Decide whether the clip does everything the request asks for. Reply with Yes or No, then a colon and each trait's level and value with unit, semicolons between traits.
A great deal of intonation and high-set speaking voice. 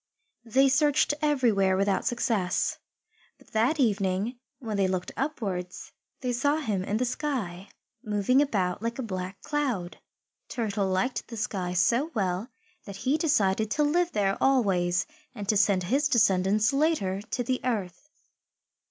Yes: wide, 5.7 semitones; high, 215 Hz